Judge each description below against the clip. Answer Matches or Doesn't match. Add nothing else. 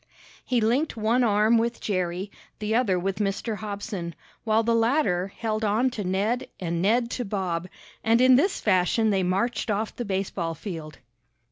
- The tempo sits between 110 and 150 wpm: Doesn't match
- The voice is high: Matches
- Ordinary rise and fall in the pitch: Matches